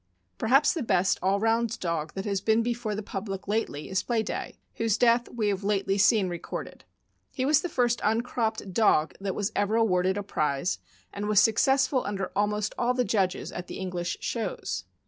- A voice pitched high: Yes, high, 210 Hz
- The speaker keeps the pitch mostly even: No, average, 3.2 semitones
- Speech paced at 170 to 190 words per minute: Yes, average, 185 wpm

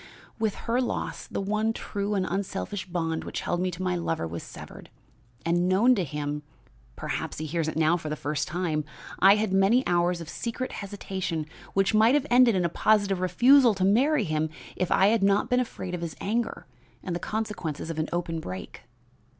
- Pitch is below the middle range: No, medium, 185 Hz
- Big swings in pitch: No, average, 4.5 semitones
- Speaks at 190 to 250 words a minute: Yes, average, 200 wpm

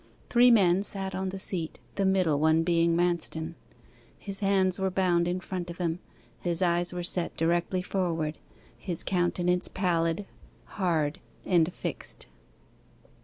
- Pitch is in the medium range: Yes, medium, 175 Hz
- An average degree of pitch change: No, narrow, 2.1 semitones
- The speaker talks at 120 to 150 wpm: Yes, average, 140 wpm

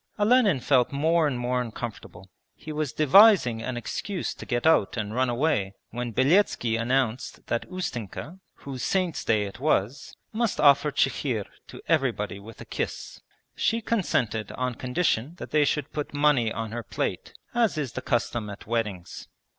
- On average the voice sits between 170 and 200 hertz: No, low, 130 Hz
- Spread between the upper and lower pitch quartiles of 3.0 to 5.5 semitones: Yes, average, 5.2 semitones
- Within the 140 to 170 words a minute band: Yes, average, 160 wpm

